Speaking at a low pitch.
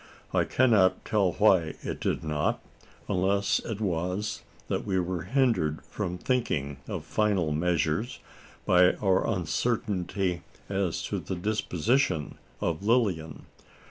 Yes: very low, 95 Hz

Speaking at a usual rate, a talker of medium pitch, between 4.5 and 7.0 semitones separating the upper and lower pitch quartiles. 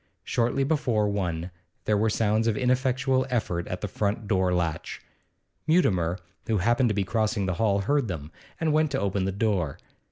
No: average, 180 wpm; low, 105 Hz; average, 5.0 semitones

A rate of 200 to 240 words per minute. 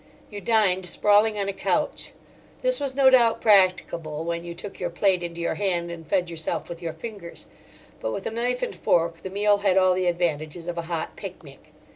Yes: fast, 205 wpm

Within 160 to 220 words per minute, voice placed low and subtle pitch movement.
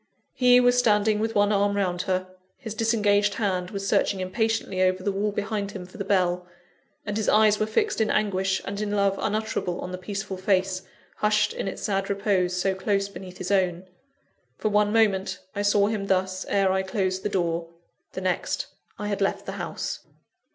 No: average, 195 wpm; high, 200 Hz; narrow, 2.0 semitones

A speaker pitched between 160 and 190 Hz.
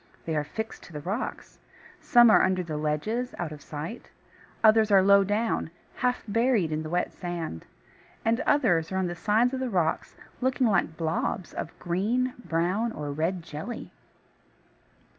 Yes: medium, 185 Hz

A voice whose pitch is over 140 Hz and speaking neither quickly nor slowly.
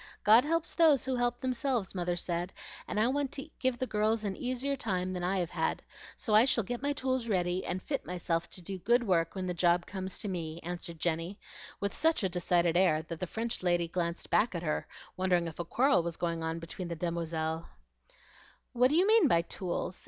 No: medium, 185 Hz; fast, 220 wpm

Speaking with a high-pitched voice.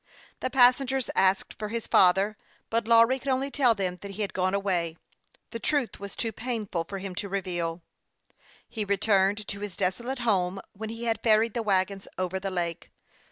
Yes: high, 200 Hz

